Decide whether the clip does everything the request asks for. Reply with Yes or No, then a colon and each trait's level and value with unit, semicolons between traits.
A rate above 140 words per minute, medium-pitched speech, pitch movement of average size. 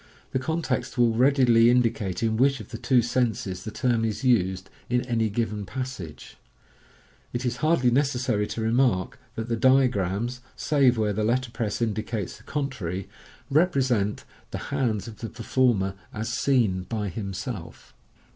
No: average, 155 wpm; low, 115 Hz; average, 3.4 semitones